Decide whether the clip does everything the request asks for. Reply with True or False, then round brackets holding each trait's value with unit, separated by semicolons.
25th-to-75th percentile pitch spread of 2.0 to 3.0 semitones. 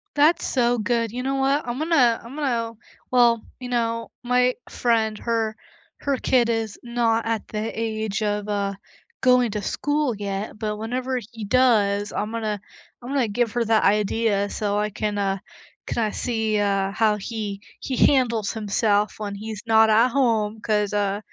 True (2.6 semitones)